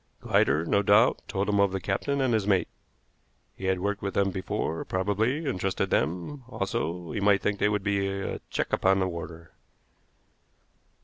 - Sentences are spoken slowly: No, average, 180 wpm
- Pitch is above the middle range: No, low, 100 Hz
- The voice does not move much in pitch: Yes, narrow, 1.7 semitones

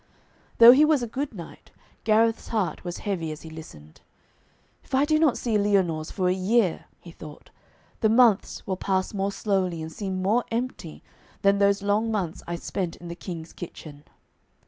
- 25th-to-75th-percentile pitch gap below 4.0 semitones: No, average, 4.7 semitones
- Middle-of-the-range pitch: No, high, 195 Hz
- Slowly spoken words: No, average, 180 wpm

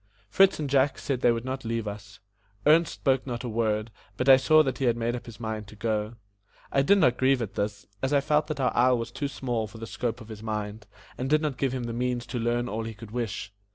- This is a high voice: No, low, 120 Hz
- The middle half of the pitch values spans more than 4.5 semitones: No, average, 3.2 semitones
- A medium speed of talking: No, fast, 260 wpm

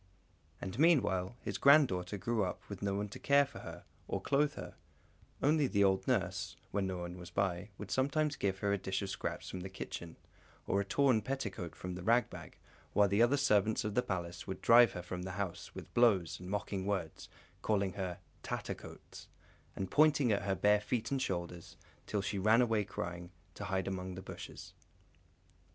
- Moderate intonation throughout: Yes, average, 4.2 semitones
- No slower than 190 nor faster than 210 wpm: Yes, average, 195 wpm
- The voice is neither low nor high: No, low, 100 Hz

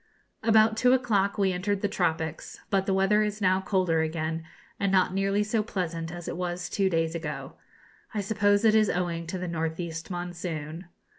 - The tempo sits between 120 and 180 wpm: No, average, 190 wpm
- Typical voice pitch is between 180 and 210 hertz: Yes, medium, 185 Hz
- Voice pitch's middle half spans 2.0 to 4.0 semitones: Yes, average, 3.5 semitones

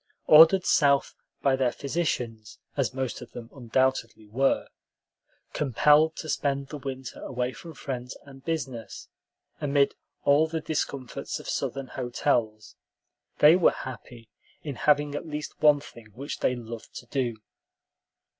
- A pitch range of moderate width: Yes, average, 3.3 semitones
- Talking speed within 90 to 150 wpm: Yes, slow, 135 wpm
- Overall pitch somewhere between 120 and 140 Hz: Yes, low, 135 Hz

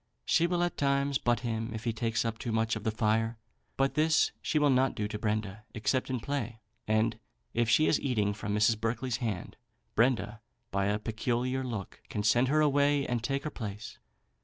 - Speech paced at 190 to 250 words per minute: Yes, average, 200 wpm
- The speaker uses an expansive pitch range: No, average, 3.7 semitones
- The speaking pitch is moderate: No, low, 115 Hz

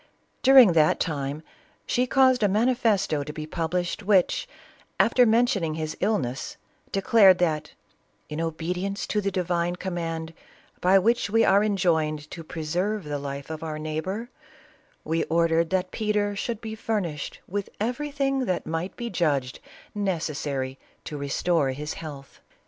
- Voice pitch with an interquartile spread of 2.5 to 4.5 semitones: No, average, 5.0 semitones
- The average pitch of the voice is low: No, medium, 175 Hz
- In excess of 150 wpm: No, average, 145 wpm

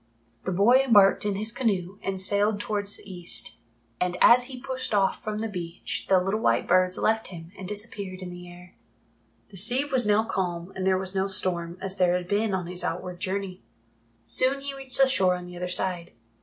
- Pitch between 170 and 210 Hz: Yes, high, 190 Hz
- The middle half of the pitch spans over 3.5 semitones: No, average, 3.1 semitones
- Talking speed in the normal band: No, fast, 210 wpm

